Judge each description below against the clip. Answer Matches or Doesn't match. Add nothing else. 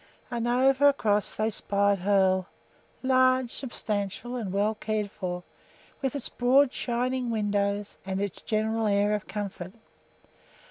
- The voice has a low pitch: Doesn't match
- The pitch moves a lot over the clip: Doesn't match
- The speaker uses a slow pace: Matches